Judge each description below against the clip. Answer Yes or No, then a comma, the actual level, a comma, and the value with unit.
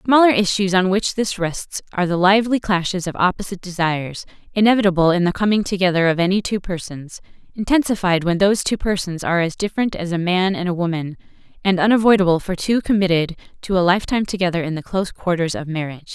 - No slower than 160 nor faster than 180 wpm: No, average, 195 wpm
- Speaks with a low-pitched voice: No, medium, 185 Hz